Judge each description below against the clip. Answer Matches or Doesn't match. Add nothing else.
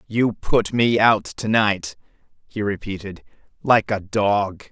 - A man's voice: Matches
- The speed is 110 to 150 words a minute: Matches